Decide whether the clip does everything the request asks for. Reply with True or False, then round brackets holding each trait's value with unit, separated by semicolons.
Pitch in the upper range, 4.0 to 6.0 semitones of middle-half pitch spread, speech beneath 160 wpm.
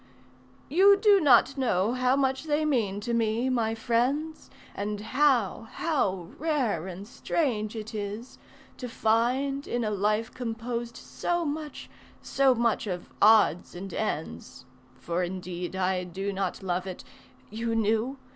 True (225 Hz; 4.9 semitones; 140 wpm)